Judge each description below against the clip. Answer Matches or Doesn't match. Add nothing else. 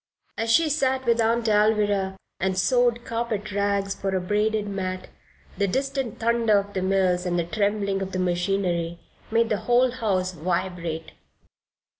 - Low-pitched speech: Doesn't match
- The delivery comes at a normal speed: Matches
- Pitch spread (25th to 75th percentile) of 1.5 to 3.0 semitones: Doesn't match